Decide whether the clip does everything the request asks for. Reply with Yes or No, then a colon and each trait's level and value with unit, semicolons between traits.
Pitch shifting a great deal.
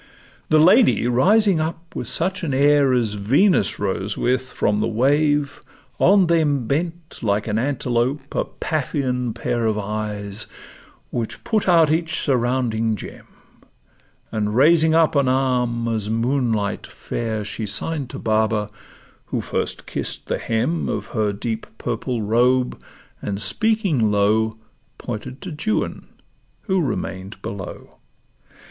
Yes: wide, 6.0 semitones